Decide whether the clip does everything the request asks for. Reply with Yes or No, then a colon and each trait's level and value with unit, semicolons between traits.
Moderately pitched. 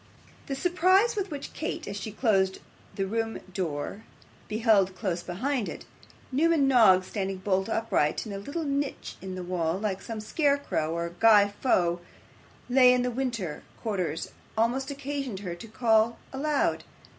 No: high, 220 Hz